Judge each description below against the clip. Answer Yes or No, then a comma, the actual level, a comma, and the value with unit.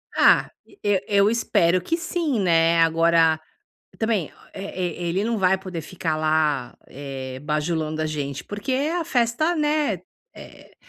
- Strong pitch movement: Yes, wide, 6.4 semitones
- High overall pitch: No, medium, 180 Hz